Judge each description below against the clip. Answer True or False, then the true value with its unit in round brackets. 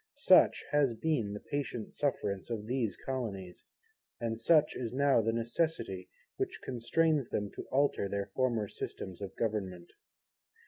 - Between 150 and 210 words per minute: False (140 wpm)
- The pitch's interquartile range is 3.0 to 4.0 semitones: False (5.0 semitones)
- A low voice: True (115 Hz)